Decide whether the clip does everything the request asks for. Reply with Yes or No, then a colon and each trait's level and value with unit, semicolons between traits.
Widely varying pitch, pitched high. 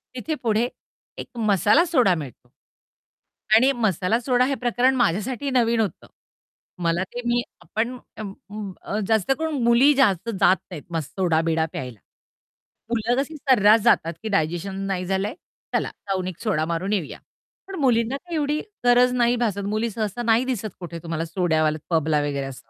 Yes: wide, 5.8 semitones; high, 215 Hz